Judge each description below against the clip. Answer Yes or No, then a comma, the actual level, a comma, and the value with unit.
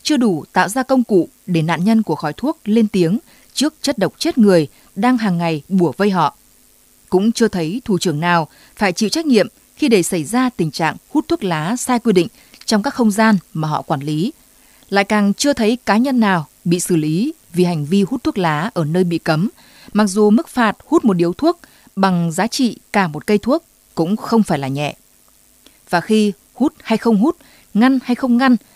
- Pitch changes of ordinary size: No, wide, 6.0 semitones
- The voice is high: Yes, high, 210 Hz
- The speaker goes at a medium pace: Yes, average, 220 wpm